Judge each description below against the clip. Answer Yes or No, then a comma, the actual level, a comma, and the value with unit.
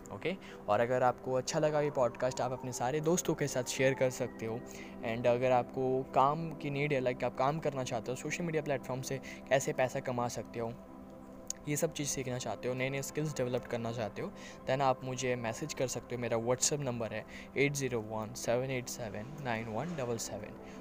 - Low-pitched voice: Yes, low, 125 Hz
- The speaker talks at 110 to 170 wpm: No, fast, 190 wpm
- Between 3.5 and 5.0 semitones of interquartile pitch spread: No, average, 2.7 semitones